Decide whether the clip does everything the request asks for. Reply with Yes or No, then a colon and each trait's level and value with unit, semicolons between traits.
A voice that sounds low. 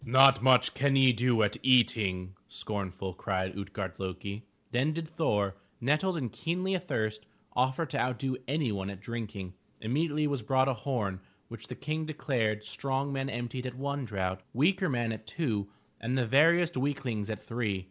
Yes: low, 125 Hz